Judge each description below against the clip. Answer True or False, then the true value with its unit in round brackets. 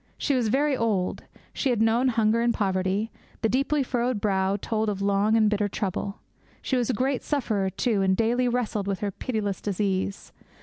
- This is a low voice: False (220 Hz)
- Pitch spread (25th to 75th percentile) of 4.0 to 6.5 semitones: False (3.6 semitones)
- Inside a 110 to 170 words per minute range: False (185 wpm)